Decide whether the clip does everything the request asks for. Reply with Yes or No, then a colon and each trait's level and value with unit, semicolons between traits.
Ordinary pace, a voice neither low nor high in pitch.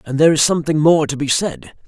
No: fast, 255 wpm; medium, 145 Hz